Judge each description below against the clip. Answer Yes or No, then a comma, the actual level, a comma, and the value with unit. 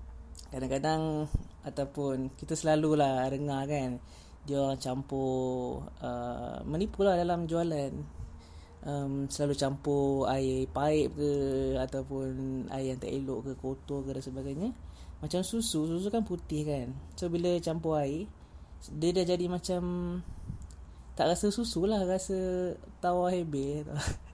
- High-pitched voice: No, medium, 140 Hz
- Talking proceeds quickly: No, average, 125 wpm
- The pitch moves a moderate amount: Yes, average, 4.3 semitones